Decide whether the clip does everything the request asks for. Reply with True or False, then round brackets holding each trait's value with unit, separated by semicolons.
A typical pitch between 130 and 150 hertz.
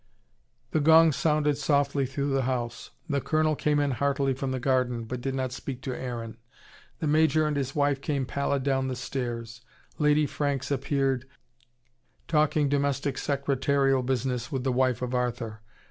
True (135 Hz)